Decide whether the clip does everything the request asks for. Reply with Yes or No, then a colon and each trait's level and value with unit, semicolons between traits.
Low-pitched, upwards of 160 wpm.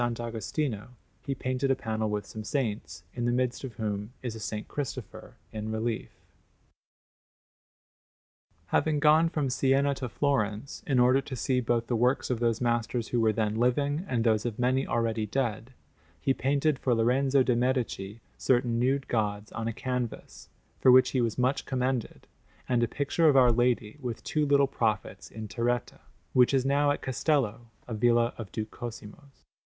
Yes: low, 120 Hz; average, 170 wpm